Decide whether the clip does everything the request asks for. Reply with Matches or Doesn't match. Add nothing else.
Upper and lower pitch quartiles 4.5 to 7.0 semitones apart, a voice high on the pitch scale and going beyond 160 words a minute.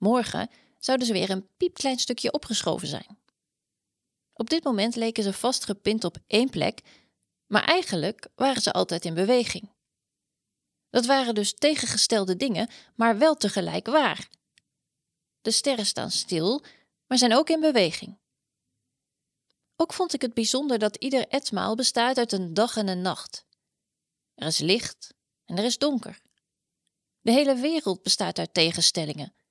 Doesn't match